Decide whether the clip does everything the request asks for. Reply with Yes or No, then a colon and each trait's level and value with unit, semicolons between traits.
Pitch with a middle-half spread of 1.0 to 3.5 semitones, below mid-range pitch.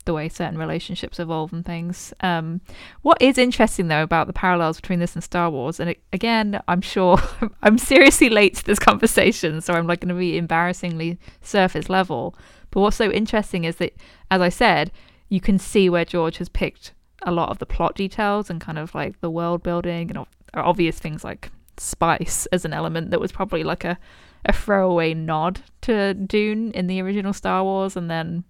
No: average, 3.0 semitones; medium, 180 Hz